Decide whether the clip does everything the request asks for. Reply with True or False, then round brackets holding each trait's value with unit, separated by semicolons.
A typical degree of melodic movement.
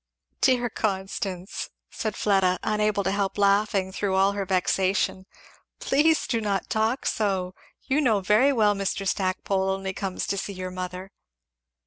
False (2.0 semitones)